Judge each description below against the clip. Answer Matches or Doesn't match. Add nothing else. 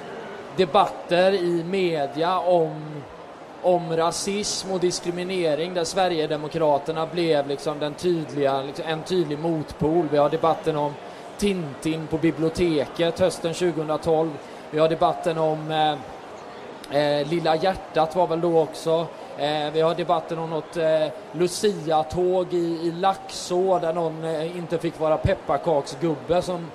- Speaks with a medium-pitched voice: Matches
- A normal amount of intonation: Doesn't match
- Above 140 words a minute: Doesn't match